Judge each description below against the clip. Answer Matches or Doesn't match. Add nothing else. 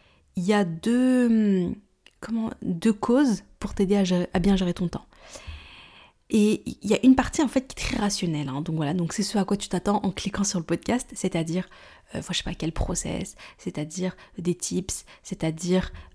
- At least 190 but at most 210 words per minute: Matches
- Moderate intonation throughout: Matches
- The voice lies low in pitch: Doesn't match